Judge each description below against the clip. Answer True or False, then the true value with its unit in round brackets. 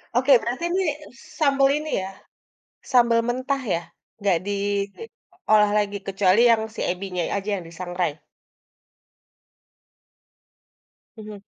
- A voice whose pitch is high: True (210 Hz)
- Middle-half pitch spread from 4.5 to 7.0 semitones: True (4.9 semitones)